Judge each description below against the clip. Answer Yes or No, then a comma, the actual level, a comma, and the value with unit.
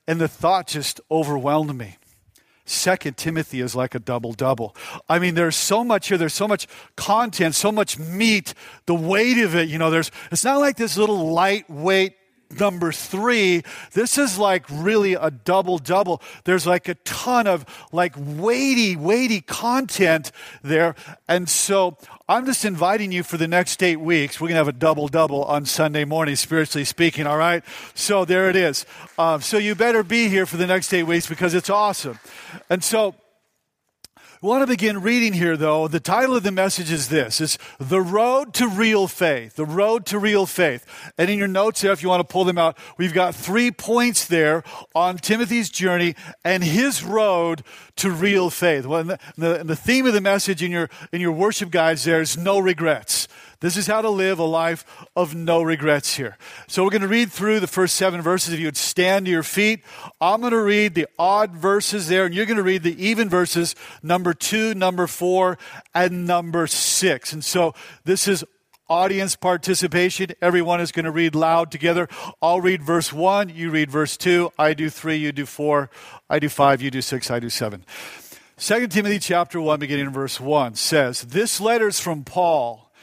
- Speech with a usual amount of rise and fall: Yes, average, 3.9 semitones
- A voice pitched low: No, medium, 175 Hz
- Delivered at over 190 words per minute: Yes, average, 200 wpm